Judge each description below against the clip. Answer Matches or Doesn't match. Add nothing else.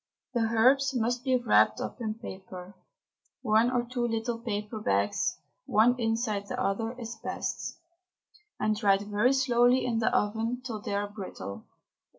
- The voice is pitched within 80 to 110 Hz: Doesn't match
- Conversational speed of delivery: Matches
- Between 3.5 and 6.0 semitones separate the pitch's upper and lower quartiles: Doesn't match